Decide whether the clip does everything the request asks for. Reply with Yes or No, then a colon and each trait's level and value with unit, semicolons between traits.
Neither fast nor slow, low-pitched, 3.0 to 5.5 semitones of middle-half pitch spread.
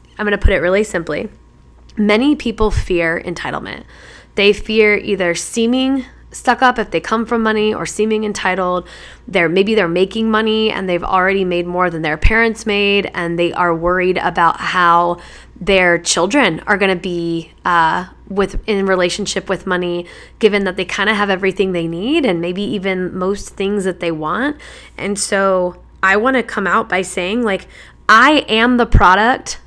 No: average, 175 wpm; high, 195 Hz; average, 3.4 semitones